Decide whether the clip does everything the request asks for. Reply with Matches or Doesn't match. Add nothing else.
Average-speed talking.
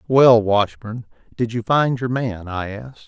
Matches